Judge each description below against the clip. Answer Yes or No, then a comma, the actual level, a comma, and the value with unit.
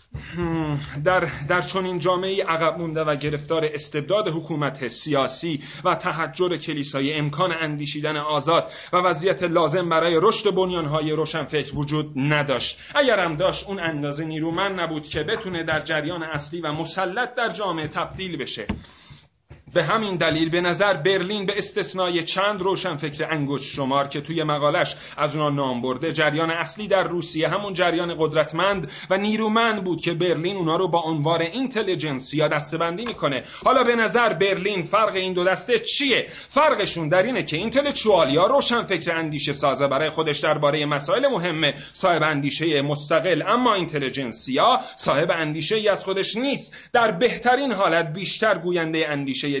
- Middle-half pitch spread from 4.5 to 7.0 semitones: No, average, 3.9 semitones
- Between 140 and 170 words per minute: Yes, average, 150 wpm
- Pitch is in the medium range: Yes, medium, 165 Hz